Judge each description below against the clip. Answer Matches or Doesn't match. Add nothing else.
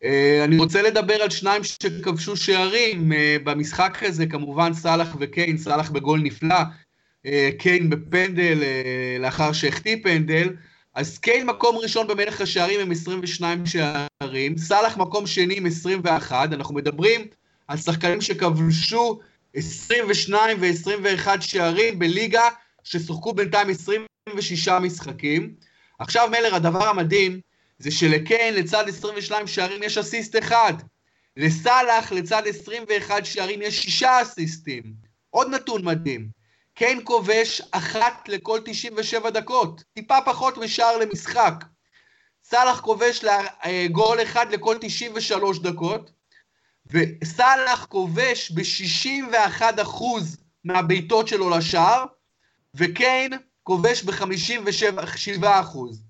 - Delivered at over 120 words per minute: Doesn't match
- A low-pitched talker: Doesn't match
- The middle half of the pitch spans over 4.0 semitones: Matches